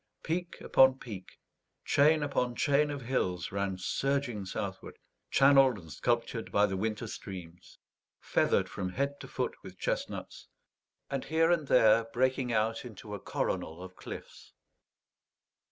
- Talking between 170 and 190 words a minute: No, slow, 135 wpm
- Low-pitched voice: Yes, low, 120 Hz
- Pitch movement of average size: No, wide, 5.8 semitones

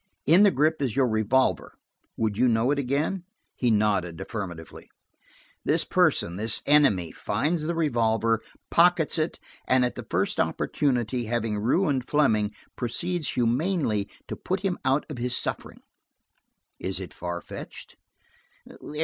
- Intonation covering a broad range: Yes, wide, 5.7 semitones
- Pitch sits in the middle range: No, low, 125 Hz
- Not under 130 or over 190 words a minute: Yes, slow, 135 wpm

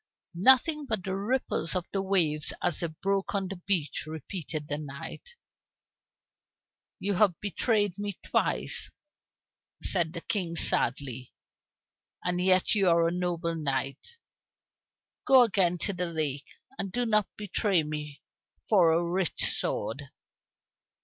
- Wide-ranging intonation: No, average, 4.1 semitones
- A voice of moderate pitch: Yes, medium, 180 Hz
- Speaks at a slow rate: Yes, slow, 130 wpm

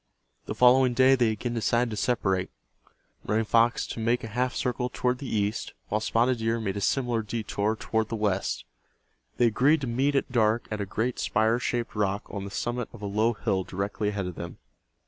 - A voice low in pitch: Yes, low, 115 Hz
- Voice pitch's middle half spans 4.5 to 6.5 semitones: No, average, 2.8 semitones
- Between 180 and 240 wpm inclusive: Yes, average, 200 wpm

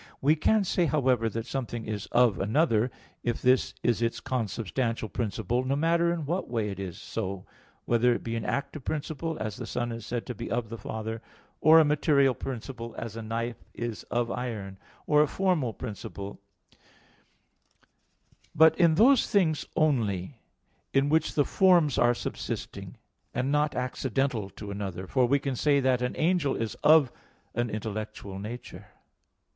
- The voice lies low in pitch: Yes, low, 120 Hz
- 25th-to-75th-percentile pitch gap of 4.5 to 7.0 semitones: Yes, average, 4.9 semitones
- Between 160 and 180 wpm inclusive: Yes, average, 165 wpm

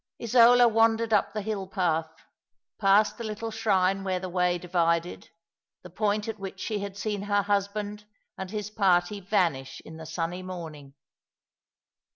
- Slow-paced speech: No, average, 155 wpm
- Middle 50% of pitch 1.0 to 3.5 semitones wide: Yes, average, 3.0 semitones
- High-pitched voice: Yes, high, 195 Hz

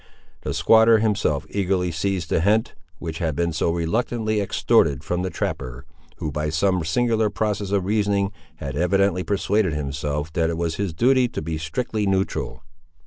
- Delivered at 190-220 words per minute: No, average, 165 wpm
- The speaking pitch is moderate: No, very low, 95 Hz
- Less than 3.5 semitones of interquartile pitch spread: No, average, 4.6 semitones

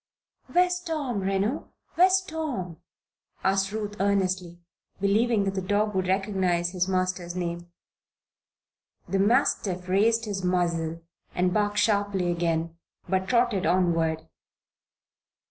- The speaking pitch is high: Yes, high, 195 Hz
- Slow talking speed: Yes, slow, 110 wpm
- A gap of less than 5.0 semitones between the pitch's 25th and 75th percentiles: Yes, average, 2.9 semitones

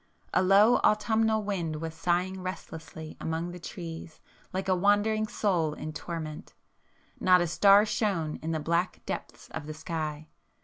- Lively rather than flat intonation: No, average, 3.8 semitones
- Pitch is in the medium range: Yes, medium, 175 Hz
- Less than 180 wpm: Yes, average, 150 wpm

